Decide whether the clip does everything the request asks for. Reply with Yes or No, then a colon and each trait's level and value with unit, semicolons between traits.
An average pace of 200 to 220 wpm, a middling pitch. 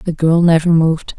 Yes: fast, 205 wpm; medium, 165 Hz